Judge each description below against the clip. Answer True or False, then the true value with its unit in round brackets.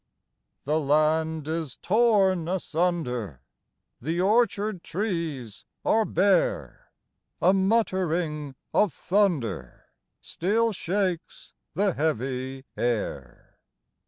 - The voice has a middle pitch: True (165 Hz)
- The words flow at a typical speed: False (80 wpm)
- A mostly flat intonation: False (5.4 semitones)